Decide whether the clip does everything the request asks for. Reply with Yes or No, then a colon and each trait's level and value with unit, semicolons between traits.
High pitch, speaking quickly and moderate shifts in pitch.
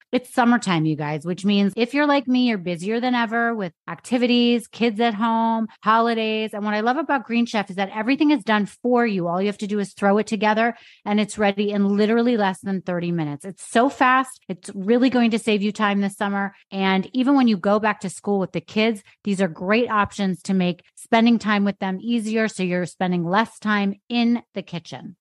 Yes: high, 210 Hz; fast, 225 wpm; average, 3.3 semitones